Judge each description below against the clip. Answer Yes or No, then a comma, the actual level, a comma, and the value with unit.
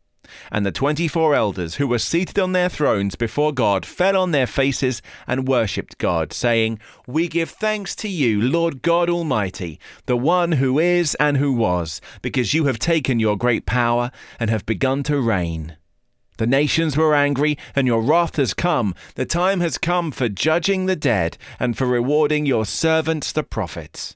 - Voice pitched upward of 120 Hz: Yes, low, 135 Hz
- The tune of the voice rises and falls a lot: Yes, wide, 5.9 semitones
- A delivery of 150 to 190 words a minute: Yes, average, 180 wpm